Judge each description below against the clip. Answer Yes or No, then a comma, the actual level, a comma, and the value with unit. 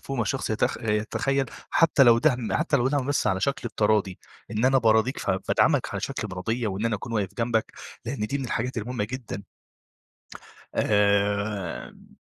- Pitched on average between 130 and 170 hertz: No, low, 115 Hz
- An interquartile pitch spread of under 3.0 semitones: No, average, 3.7 semitones